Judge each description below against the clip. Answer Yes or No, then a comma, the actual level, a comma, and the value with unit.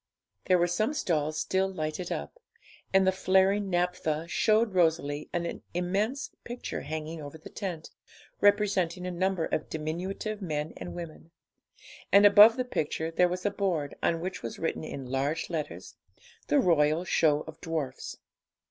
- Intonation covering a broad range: No, average, 3.6 semitones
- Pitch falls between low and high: Yes, medium, 175 Hz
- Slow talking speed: No, average, 155 wpm